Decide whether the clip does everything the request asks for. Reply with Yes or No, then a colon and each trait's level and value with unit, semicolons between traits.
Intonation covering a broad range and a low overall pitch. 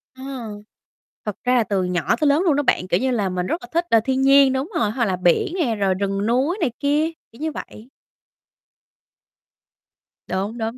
No: wide, 6.1 semitones; high, 240 Hz